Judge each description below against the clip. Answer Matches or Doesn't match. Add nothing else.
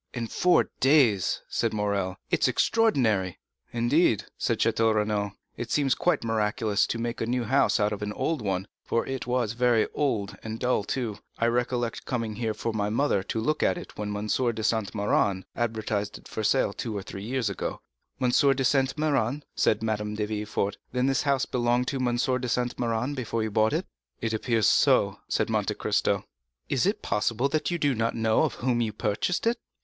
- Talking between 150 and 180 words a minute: Doesn't match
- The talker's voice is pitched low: Matches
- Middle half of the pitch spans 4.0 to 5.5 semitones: Doesn't match